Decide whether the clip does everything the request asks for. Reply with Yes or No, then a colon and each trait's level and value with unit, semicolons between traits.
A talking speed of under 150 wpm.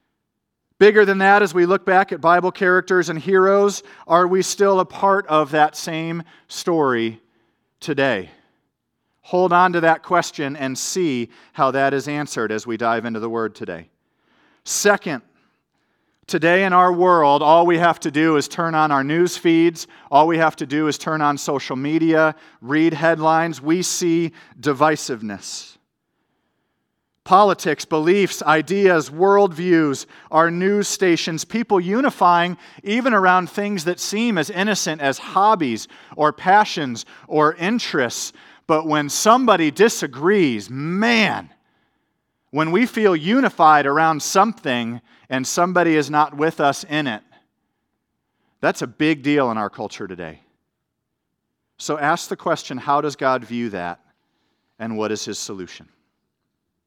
Yes: average, 140 wpm